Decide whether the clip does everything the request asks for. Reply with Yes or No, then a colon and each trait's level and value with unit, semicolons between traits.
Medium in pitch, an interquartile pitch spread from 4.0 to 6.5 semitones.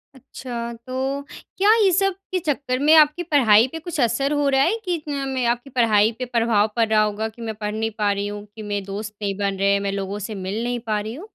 No: high, 235 Hz; average, 5.1 semitones